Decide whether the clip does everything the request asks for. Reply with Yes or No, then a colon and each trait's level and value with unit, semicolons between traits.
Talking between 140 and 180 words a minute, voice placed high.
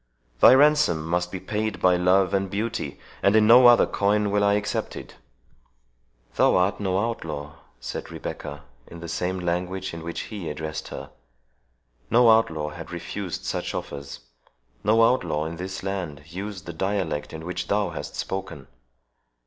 No: average, 160 wpm; very low, 95 Hz